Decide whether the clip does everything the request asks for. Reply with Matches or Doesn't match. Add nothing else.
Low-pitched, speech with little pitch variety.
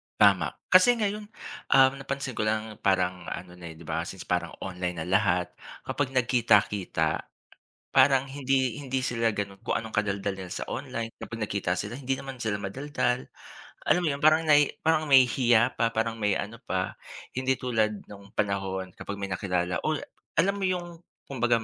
Doesn't match